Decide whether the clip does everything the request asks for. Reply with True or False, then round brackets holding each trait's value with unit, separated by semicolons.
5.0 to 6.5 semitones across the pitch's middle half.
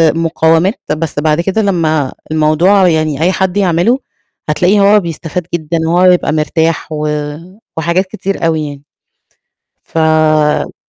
False (2.9 semitones)